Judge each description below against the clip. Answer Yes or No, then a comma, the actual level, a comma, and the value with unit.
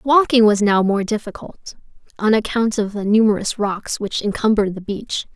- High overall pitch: Yes, high, 210 Hz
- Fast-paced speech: No, average, 170 wpm